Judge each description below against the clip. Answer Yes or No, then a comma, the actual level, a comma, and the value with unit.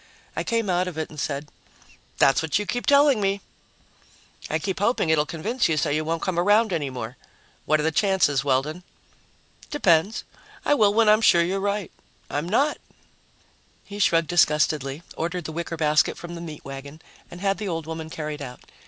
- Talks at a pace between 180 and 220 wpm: Yes, average, 190 wpm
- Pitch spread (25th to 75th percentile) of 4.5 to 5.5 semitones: Yes, average, 4.8 semitones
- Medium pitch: Yes, medium, 170 Hz